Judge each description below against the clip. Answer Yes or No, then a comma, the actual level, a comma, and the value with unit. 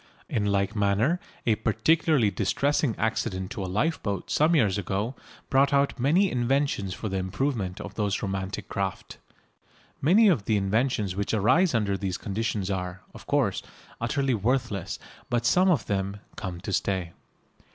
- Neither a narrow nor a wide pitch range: No, wide, 5.7 semitones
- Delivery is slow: No, average, 150 wpm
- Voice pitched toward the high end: No, low, 105 Hz